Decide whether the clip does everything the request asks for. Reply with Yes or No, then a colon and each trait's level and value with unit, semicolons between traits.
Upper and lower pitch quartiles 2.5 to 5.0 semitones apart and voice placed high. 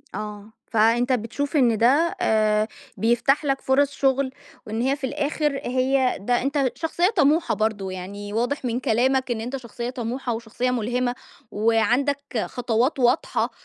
Yes: average, 3.4 semitones; high, 245 Hz